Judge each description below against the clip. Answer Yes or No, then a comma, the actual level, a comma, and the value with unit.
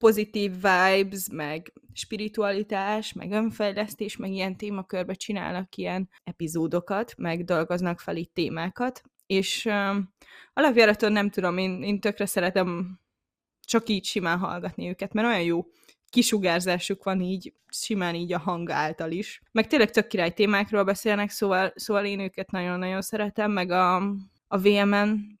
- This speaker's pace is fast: No, average, 140 wpm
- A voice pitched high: Yes, high, 195 Hz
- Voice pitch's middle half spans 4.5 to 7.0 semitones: No, narrow, 2.5 semitones